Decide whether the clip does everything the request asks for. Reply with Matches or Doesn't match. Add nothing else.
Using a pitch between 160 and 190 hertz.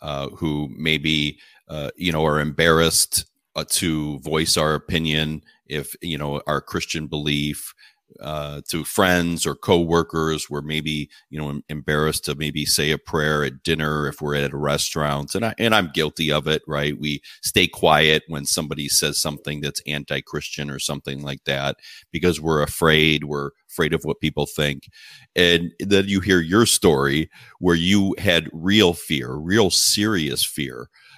Doesn't match